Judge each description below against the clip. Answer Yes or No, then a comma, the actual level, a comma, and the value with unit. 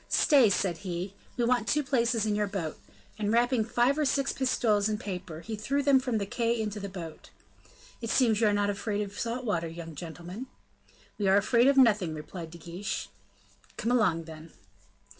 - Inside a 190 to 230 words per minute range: Yes, average, 195 wpm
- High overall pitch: Yes, high, 210 Hz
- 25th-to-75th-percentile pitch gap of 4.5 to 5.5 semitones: Yes, average, 4.8 semitones